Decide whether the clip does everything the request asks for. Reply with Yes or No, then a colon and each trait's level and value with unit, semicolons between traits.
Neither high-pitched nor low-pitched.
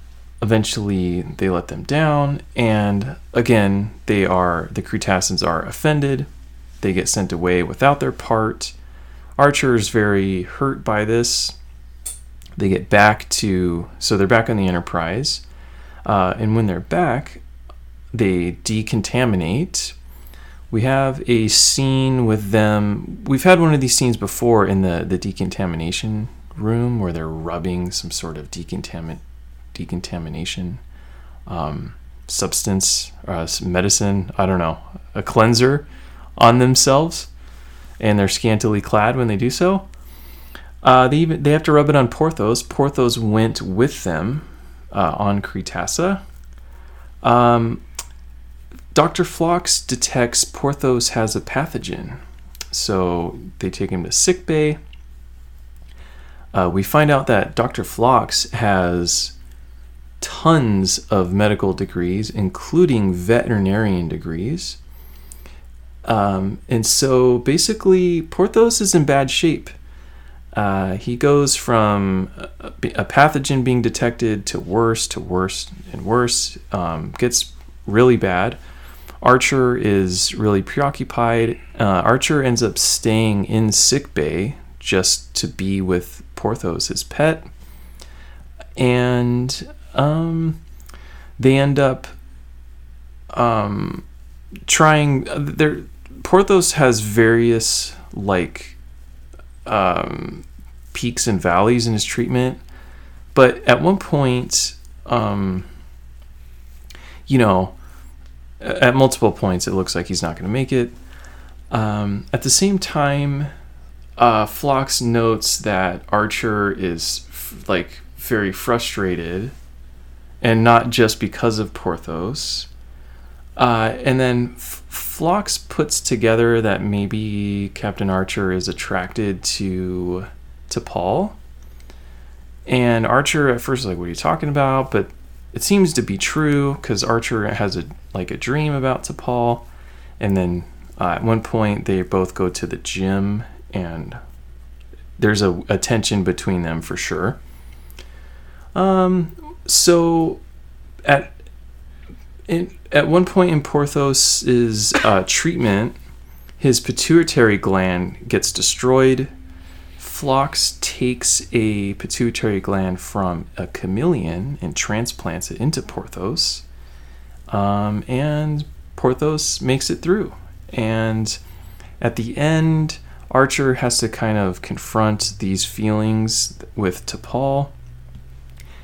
No: low, 100 Hz